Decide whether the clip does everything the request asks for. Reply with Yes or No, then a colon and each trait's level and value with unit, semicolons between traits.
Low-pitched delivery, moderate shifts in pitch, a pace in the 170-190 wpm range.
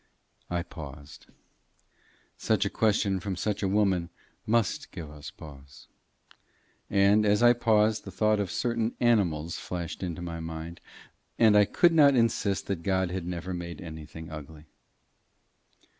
No: very low, 95 Hz; average, 4.4 semitones; average, 145 wpm